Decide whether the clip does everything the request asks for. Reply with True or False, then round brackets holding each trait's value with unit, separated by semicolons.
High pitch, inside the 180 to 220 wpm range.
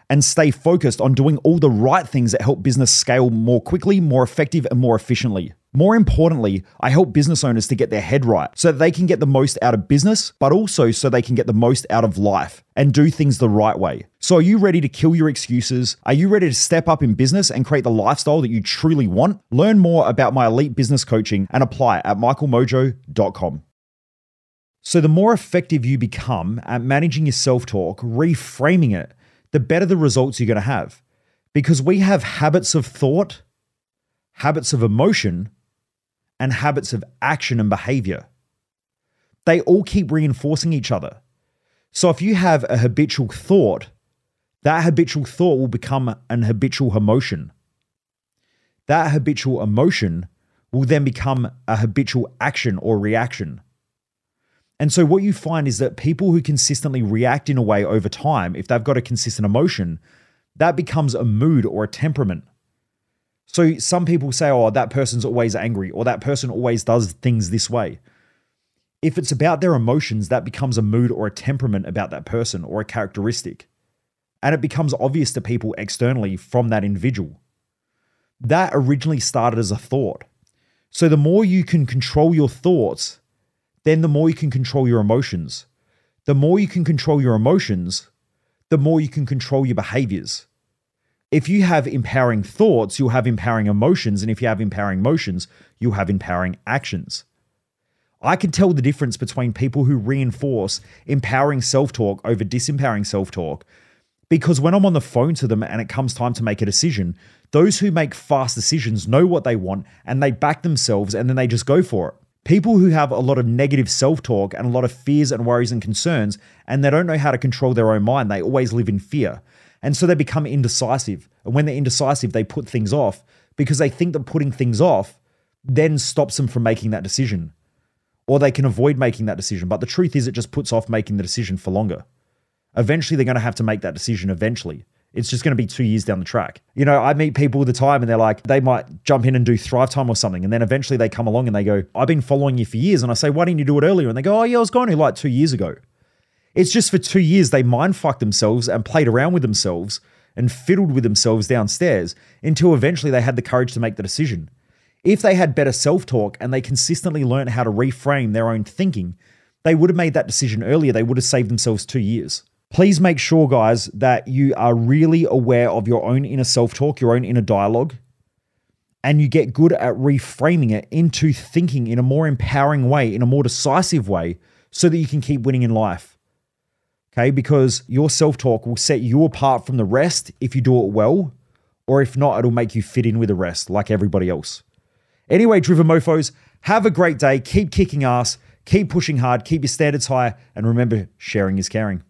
False (130 Hz; 205 wpm)